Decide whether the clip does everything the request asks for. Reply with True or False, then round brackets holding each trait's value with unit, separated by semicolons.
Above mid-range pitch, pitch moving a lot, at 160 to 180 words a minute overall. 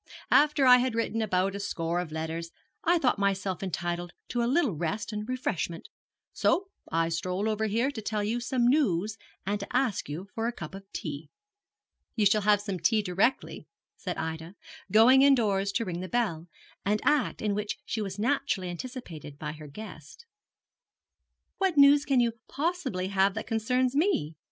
True (210 Hz; 5.8 semitones; 175 wpm)